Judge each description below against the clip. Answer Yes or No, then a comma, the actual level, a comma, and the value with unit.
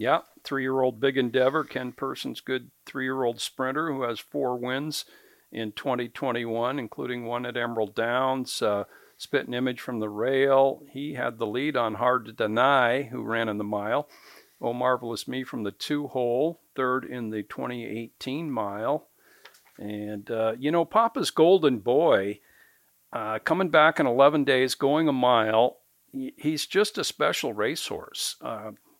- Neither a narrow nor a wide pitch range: Yes, average, 3.0 semitones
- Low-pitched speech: Yes, low, 130 Hz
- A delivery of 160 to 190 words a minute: No, average, 150 wpm